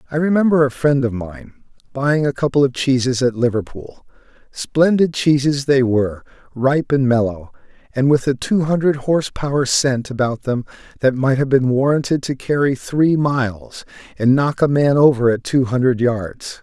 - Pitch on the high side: No, low, 135 Hz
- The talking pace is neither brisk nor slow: Yes, average, 175 wpm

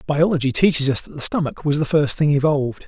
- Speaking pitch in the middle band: Yes, medium, 145 Hz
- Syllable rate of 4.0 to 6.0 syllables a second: No, 6.2 syllables/s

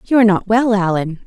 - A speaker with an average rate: No, fast, 235 wpm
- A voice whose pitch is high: Yes, high, 205 Hz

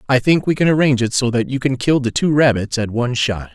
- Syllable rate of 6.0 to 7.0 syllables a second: Yes, 6.3 syllables/s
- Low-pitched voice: Yes, low, 125 Hz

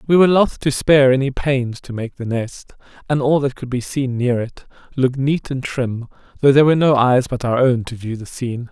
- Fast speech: Yes, fast, 240 wpm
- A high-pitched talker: No, low, 130 Hz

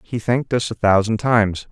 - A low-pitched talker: Yes, low, 110 Hz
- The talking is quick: Yes, fast, 210 wpm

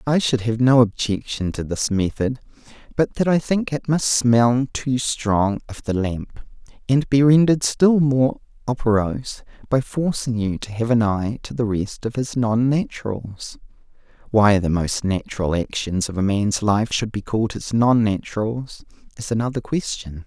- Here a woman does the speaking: No, male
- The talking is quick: No, average, 165 wpm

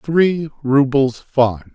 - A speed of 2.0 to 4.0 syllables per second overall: Yes, 2.5 syllables/s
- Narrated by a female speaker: No, male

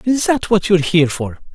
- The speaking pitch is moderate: Yes, medium, 180 Hz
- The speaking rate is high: Yes, fast, 235 wpm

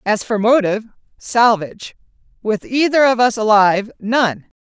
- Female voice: Yes, female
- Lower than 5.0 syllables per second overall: Yes, 4.8 syllables/s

